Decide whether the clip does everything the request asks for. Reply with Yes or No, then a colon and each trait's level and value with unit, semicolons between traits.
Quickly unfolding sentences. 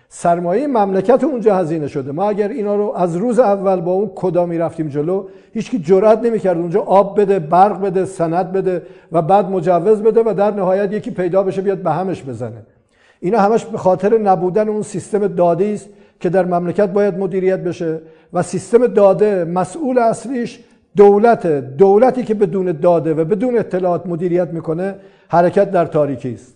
Yes: fast, 175 wpm